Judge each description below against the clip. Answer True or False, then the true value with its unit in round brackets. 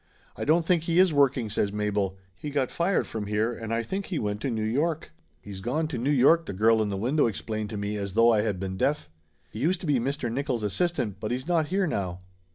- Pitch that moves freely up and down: True (6.4 semitones)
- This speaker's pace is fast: True (250 wpm)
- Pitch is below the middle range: True (120 Hz)